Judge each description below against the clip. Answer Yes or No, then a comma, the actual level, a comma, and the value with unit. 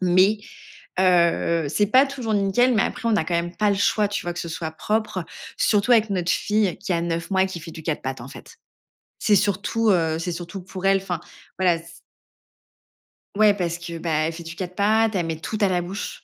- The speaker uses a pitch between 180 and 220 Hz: Yes, medium, 185 Hz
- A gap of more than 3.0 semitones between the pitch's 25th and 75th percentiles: Yes, average, 3.6 semitones